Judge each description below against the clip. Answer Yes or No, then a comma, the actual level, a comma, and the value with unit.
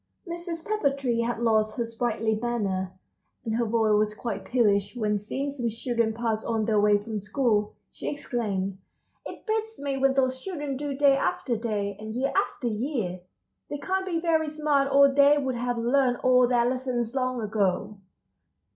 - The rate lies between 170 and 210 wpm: Yes, average, 175 wpm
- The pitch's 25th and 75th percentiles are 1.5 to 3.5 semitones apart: No, average, 4.3 semitones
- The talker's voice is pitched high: Yes, high, 240 Hz